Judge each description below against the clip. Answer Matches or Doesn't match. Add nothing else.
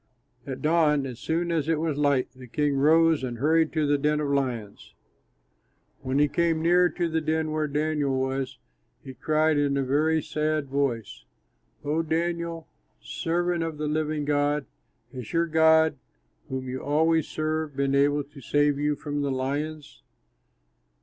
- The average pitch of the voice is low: Doesn't match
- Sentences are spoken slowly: Doesn't match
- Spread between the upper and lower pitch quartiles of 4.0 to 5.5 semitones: Doesn't match